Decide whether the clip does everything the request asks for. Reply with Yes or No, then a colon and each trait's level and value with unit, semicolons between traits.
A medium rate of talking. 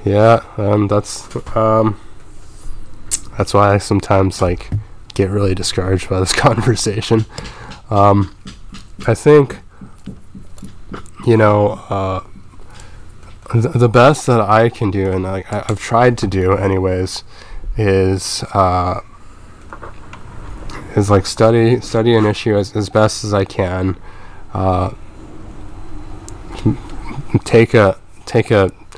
No: slow, 115 wpm